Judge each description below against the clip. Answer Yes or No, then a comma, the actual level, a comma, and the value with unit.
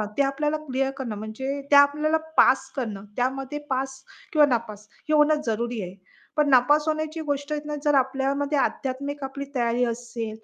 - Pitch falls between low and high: No, very high, 270 Hz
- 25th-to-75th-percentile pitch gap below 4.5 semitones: Yes, average, 3.3 semitones